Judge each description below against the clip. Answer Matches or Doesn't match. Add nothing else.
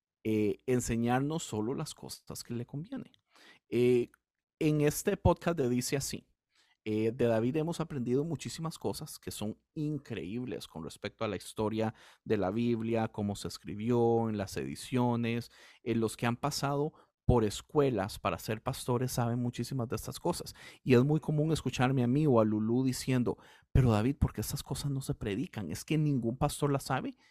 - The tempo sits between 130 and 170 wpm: Doesn't match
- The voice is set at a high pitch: Doesn't match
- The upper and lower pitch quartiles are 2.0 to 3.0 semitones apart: Doesn't match